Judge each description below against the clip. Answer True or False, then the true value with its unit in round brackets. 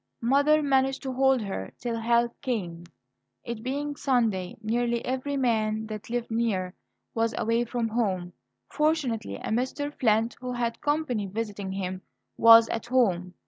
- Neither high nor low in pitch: False (230 Hz)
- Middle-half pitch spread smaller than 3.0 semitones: False (3.3 semitones)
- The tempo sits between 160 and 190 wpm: False (145 wpm)